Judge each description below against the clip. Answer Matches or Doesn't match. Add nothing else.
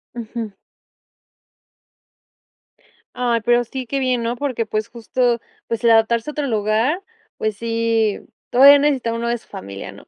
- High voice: Matches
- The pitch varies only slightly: Matches